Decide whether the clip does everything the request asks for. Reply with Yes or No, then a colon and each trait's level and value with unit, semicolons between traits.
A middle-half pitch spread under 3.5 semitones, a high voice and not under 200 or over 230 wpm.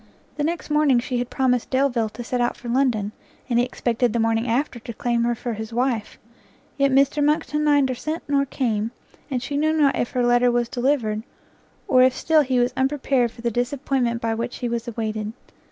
Yes: average, 2.8 semitones; high, 245 Hz; fast, 205 wpm